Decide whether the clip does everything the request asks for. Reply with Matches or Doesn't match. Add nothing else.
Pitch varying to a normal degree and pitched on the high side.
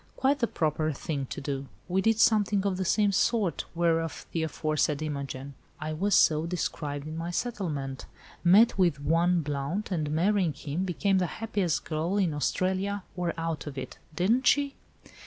Doesn't match